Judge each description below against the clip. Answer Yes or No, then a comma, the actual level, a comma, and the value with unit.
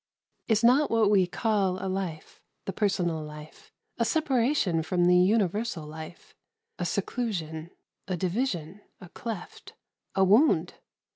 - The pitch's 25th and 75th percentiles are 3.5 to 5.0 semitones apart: Yes, average, 4.7 semitones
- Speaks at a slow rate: Yes, slow, 130 wpm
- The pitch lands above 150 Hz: Yes, high, 190 Hz